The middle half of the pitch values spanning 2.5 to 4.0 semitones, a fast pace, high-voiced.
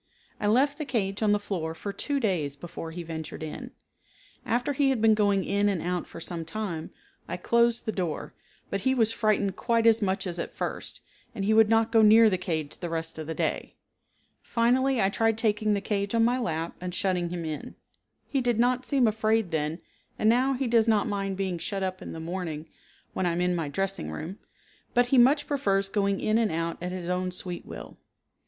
No: average, 4.5 semitones; fast, 215 wpm; high, 200 Hz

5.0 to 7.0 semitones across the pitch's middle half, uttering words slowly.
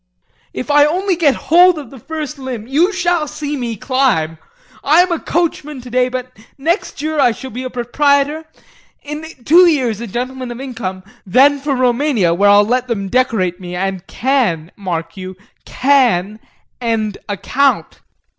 No: wide, 5.6 semitones; average, 165 wpm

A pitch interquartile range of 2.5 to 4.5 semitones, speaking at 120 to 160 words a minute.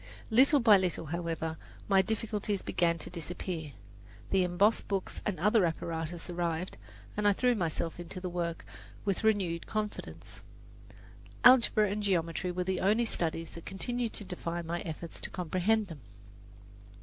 Yes: average, 3.8 semitones; average, 150 wpm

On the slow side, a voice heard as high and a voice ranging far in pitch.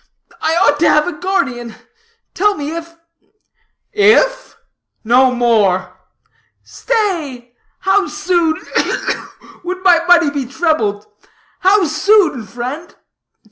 Yes: slow, 115 wpm; very high, 320 Hz; wide, 6.7 semitones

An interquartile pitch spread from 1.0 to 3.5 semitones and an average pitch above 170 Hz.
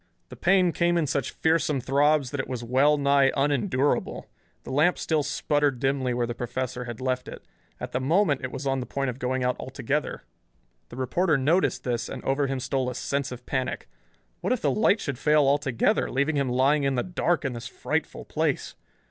No: average, 2.7 semitones; low, 135 Hz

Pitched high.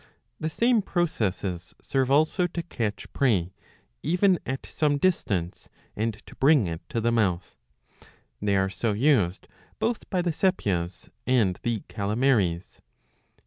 No: low, 115 Hz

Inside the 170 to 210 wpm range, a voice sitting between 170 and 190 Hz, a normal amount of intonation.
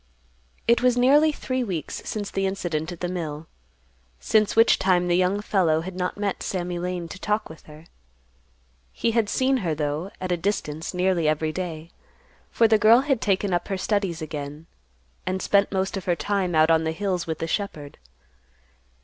Yes: average, 185 wpm; medium, 185 Hz; average, 4.0 semitones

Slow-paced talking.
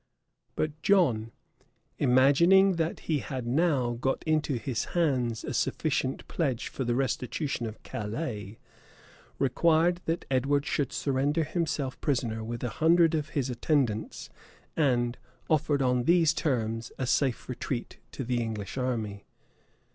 Yes: slow, 130 wpm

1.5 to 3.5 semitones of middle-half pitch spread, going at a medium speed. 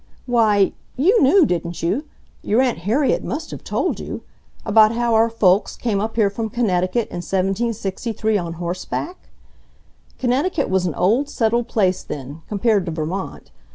No: average, 4.6 semitones; average, 145 wpm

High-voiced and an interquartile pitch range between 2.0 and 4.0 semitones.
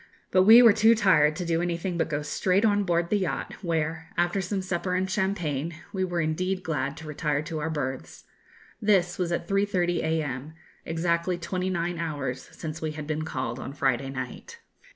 No: medium, 170 Hz; average, 3.4 semitones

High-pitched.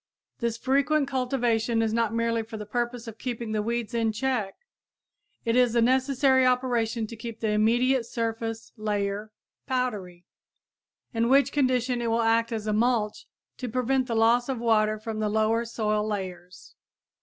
Yes: high, 230 Hz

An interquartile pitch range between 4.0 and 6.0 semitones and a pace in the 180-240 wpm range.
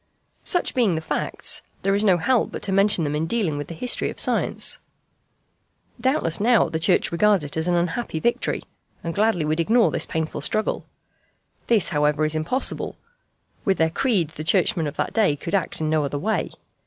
Yes: wide, 5.4 semitones; average, 190 wpm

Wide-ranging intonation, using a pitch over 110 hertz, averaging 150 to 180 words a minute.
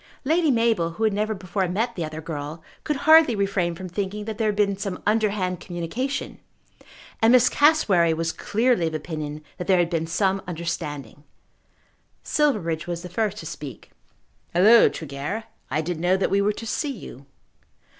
No: average, 4.9 semitones; high, 190 Hz; average, 175 wpm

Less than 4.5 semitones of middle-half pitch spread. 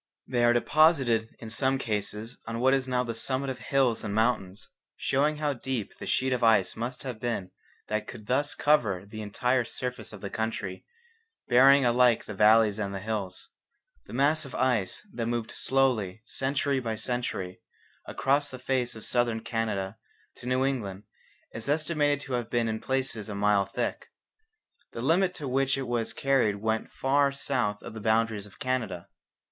Yes: average, 3.6 semitones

